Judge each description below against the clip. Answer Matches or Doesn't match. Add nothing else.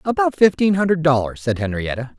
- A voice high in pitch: Doesn't match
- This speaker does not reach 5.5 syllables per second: Doesn't match